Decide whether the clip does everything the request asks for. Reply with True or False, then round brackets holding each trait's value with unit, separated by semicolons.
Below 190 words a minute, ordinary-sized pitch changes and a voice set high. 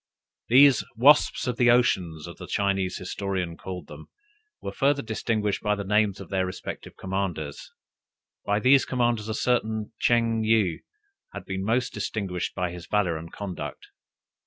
False (160 wpm; 3.9 semitones; 105 Hz)